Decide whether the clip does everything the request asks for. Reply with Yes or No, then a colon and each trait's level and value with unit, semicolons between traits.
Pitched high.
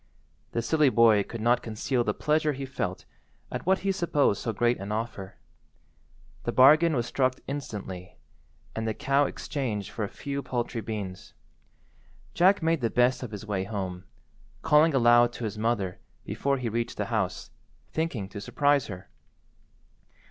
No: low, 120 Hz